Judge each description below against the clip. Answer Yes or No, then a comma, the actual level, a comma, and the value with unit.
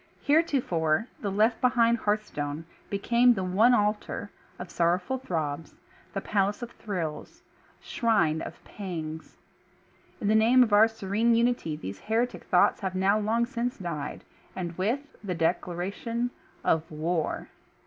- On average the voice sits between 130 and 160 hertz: No, high, 205 Hz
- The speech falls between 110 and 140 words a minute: Yes, slow, 135 wpm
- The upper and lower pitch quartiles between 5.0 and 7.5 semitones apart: Yes, wide, 5.4 semitones